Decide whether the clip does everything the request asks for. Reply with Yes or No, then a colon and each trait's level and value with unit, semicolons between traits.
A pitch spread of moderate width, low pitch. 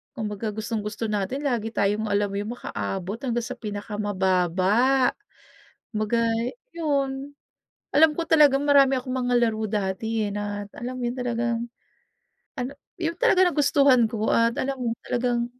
No: average, 4.3 semitones; high, 235 Hz